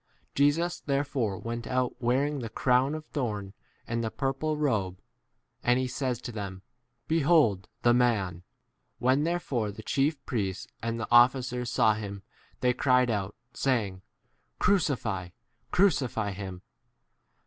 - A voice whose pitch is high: No, low, 125 Hz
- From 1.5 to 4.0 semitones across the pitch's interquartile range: No, average, 4.7 semitones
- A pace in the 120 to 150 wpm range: Yes, slow, 135 wpm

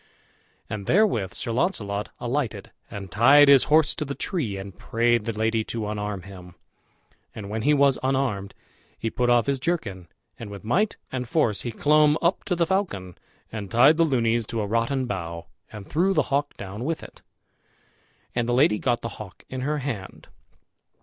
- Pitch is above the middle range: No, low, 120 Hz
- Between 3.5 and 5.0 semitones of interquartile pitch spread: No, wide, 5.6 semitones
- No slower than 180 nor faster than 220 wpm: Yes, average, 185 wpm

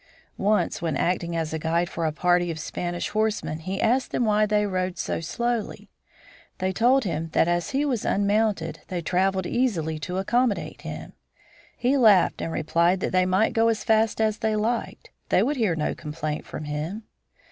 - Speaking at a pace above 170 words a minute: Yes, average, 185 wpm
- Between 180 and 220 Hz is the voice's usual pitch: Yes, medium, 185 Hz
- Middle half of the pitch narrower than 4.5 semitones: No, average, 4.8 semitones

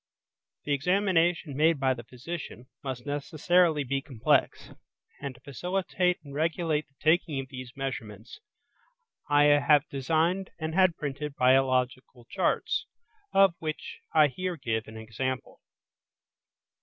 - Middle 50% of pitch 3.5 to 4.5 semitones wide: Yes, average, 4.1 semitones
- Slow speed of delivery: Yes, slow, 125 wpm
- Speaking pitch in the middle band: Yes, medium, 145 Hz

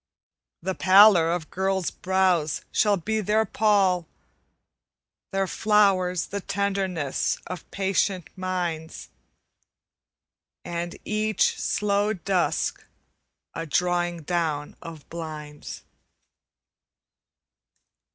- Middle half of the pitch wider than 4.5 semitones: No, average, 3.0 semitones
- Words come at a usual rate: No, slow, 85 wpm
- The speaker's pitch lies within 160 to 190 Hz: Yes, medium, 185 Hz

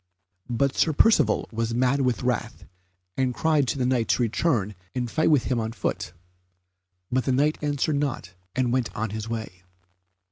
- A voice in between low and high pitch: No, low, 125 Hz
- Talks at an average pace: Yes, average, 175 wpm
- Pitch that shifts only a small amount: No, average, 3.5 semitones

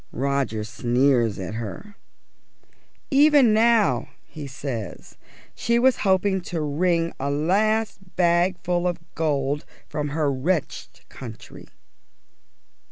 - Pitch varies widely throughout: Yes, wide, 6.1 semitones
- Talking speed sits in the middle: No, slow, 105 wpm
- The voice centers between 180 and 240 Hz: No, medium, 160 Hz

